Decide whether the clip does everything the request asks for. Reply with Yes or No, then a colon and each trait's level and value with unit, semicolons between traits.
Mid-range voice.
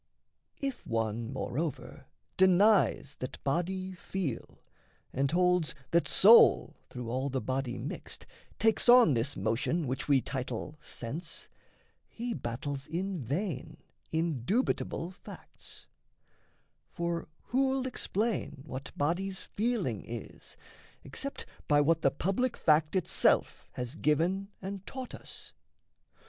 Yes: medium, 165 Hz